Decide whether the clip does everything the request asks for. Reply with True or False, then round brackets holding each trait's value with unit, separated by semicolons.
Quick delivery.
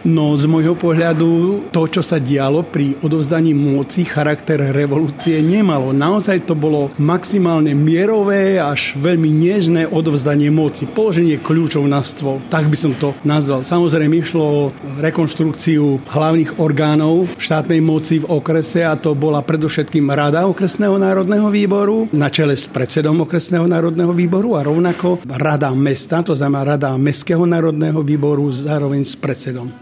False (145 wpm)